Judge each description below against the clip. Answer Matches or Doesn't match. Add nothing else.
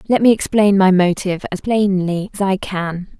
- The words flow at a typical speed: Matches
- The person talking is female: Matches